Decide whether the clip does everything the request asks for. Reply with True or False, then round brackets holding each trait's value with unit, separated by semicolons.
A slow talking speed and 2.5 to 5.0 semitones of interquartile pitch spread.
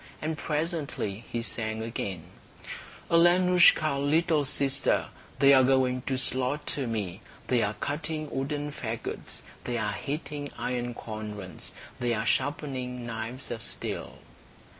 True (120 wpm; 4.3 semitones)